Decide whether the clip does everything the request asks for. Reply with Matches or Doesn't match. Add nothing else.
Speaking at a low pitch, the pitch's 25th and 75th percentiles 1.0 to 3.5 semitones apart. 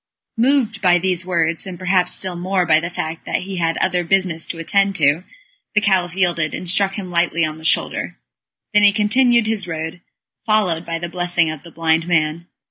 Doesn't match